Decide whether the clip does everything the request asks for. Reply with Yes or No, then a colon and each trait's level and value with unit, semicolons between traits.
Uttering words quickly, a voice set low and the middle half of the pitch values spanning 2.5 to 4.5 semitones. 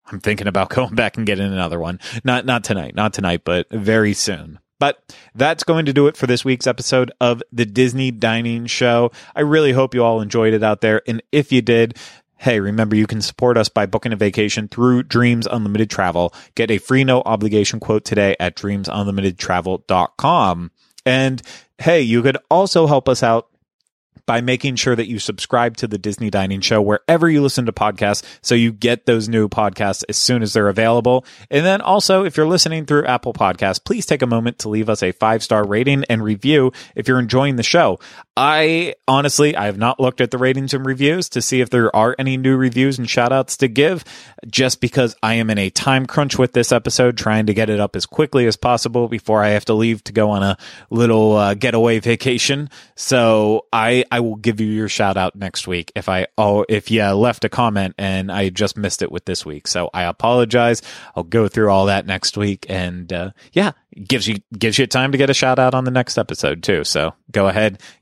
Yes: fast, 215 wpm; low, 115 Hz; average, 3.5 semitones